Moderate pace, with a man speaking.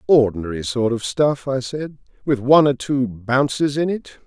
Yes: average, 185 wpm; male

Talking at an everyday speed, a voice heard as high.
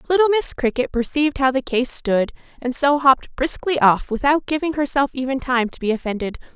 Yes: average, 190 wpm; very high, 270 Hz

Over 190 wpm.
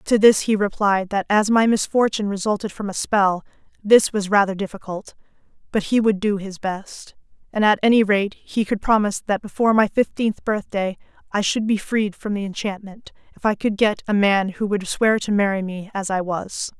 Yes: average, 200 wpm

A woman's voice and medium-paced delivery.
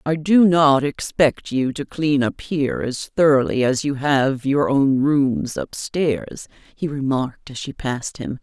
Yes: female; average, 180 wpm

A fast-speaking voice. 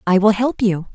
Yes: fast, 255 wpm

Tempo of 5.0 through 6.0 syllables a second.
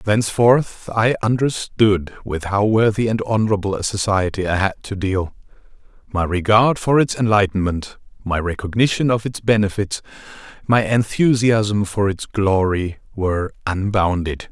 No: 4.6 syllables/s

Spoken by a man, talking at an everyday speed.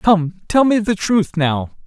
Yes: male; average, 160 wpm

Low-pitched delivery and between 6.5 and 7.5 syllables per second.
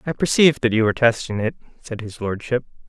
Yes: low, 120 Hz; 6.6 syllables/s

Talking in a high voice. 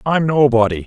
No: low, 130 Hz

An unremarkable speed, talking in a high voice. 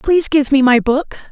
No: fast, 230 wpm; very high, 280 Hz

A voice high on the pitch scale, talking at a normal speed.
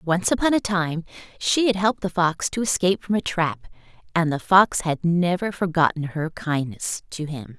No: medium, 175 Hz; average, 190 wpm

